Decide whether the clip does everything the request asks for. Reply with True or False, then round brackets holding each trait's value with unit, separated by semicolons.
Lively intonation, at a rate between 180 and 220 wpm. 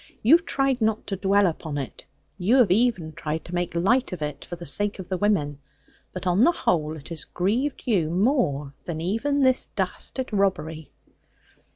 True (6.3 semitones; 190 wpm)